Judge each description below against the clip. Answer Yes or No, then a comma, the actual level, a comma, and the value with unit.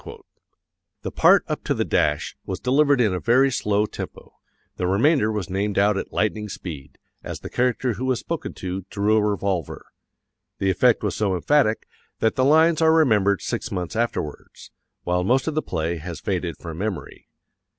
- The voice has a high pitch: No, low, 105 Hz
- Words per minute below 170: No, average, 180 wpm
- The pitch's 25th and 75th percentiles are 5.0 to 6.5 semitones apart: Yes, wide, 5.5 semitones